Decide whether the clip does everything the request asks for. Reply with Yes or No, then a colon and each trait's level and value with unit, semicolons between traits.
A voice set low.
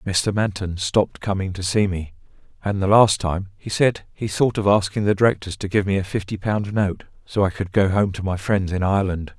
Yes: low, 100 Hz